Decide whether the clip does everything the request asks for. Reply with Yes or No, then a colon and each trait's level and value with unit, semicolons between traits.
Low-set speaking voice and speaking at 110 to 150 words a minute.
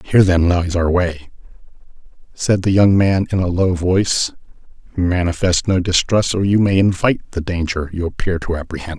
No: very low, 90 Hz; average, 175 wpm